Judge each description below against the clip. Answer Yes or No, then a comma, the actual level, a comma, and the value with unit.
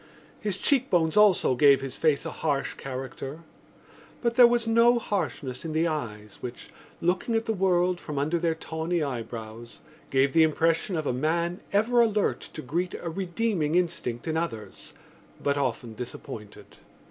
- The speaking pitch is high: No, medium, 160 Hz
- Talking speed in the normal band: Yes, average, 160 wpm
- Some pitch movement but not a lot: No, wide, 5.7 semitones